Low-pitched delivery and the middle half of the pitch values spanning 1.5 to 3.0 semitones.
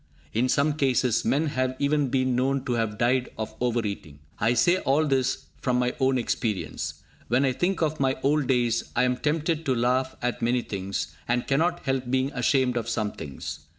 Yes: low, 130 Hz; narrow, 2.5 semitones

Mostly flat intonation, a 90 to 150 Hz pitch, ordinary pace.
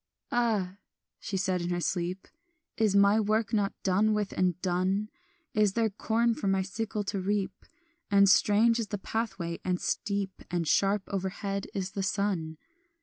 No: narrow, 2.2 semitones; high, 200 Hz; average, 160 wpm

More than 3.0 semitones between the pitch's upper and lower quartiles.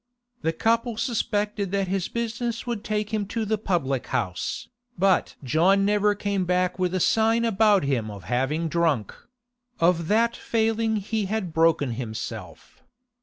Yes: average, 5.1 semitones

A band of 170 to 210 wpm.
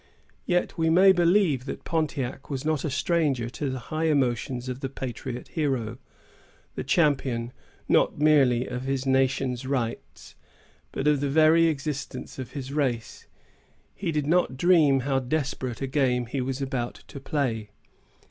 No: average, 155 wpm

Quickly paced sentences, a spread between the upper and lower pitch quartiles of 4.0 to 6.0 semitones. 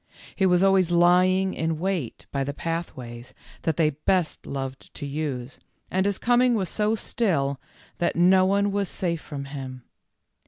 No: average, 160 wpm; average, 5.3 semitones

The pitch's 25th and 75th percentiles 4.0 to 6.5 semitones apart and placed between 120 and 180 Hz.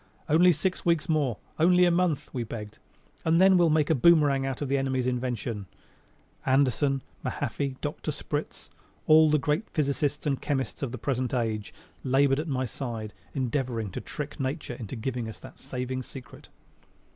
No: average, 3.4 semitones; low, 135 Hz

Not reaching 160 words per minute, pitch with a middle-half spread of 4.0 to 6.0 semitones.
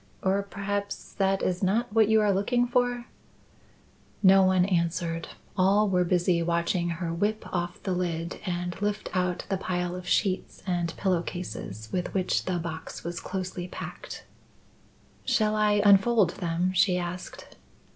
No: average, 150 wpm; narrow, 2.5 semitones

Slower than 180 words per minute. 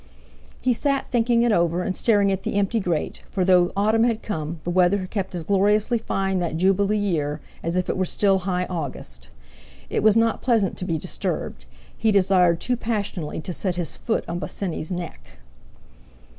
No: average, 185 wpm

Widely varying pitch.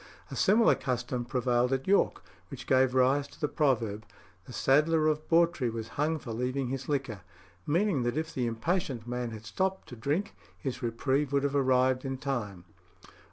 No: average, 3.6 semitones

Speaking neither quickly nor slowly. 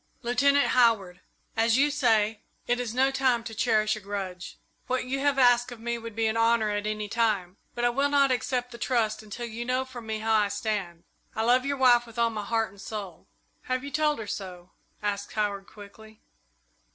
No: fast, 210 wpm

